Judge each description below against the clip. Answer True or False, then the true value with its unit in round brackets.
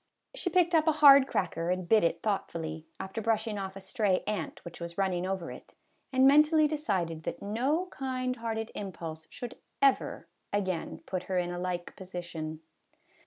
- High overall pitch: True (195 Hz)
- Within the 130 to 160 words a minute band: False (170 wpm)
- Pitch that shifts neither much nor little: False (6.7 semitones)